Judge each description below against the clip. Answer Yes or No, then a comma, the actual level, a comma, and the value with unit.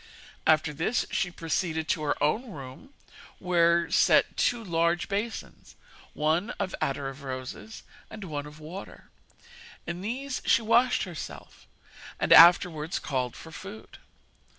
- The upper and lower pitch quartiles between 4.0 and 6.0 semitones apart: Yes, average, 4.8 semitones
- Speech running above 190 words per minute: No, slow, 135 wpm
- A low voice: No, medium, 170 Hz